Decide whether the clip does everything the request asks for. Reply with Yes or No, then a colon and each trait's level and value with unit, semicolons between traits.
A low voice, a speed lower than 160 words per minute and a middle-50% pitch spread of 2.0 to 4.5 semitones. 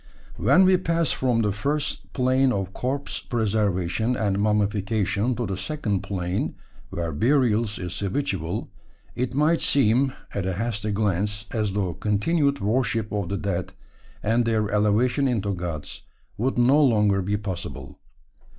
Yes: low, 105 Hz; average, 140 wpm; average, 4.2 semitones